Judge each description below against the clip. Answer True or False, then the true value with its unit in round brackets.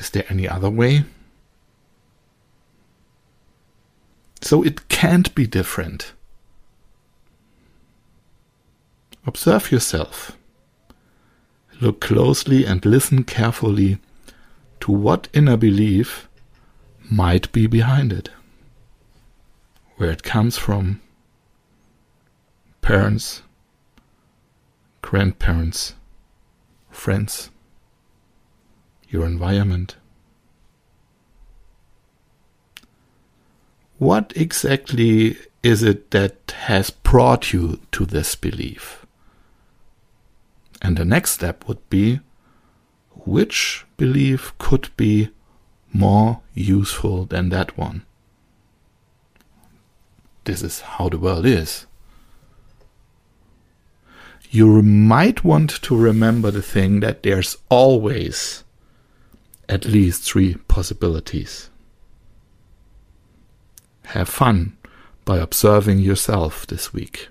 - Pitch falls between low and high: False (105 Hz)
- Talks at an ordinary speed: False (80 wpm)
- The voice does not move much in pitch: False (3.6 semitones)